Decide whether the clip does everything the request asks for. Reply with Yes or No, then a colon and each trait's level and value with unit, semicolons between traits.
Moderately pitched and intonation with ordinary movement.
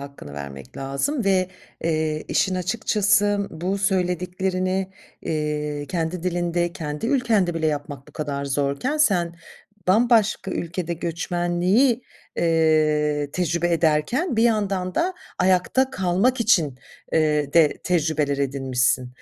Yes: medium, 175 Hz; average, 4.3 semitones